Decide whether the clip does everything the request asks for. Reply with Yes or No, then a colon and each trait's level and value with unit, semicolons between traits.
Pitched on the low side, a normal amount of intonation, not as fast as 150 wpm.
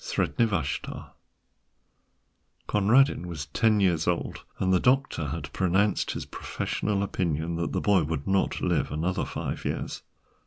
Yes: very low, 90 Hz; average, 4.1 semitones; average, 140 wpm